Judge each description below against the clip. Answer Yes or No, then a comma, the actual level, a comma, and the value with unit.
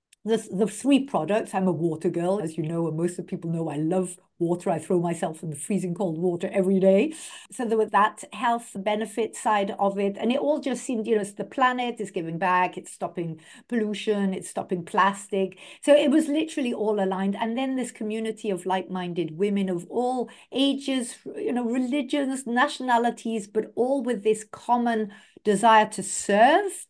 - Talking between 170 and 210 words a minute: Yes, average, 195 wpm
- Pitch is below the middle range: No, high, 210 Hz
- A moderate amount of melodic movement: Yes, average, 4.4 semitones